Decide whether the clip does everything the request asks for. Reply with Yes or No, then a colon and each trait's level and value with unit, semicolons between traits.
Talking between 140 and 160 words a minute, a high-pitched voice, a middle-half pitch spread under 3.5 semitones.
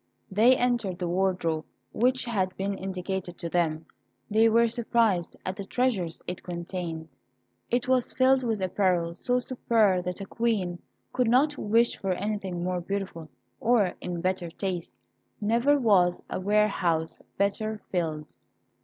No: average, 145 wpm; high, 195 Hz; average, 4.5 semitones